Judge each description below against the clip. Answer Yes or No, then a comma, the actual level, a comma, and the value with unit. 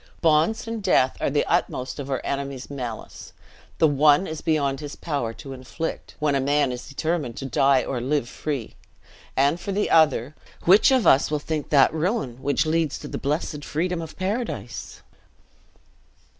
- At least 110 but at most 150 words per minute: No, average, 175 wpm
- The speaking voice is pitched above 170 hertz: No, medium, 145 Hz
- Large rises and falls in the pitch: No, average, 3.3 semitones